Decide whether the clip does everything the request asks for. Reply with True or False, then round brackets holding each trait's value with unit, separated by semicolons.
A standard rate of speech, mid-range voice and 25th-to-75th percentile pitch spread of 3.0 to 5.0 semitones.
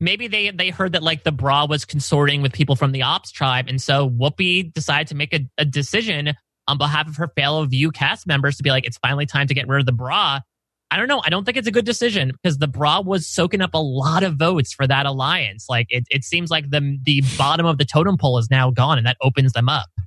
False (265 wpm; 145 Hz; 3.3 semitones)